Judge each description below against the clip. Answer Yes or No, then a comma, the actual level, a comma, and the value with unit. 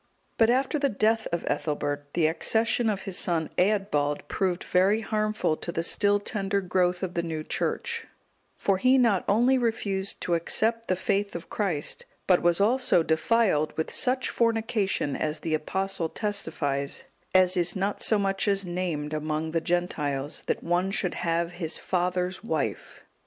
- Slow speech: No, average, 160 wpm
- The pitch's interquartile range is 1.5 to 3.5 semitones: No, average, 4.3 semitones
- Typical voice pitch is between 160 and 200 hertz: Yes, medium, 185 Hz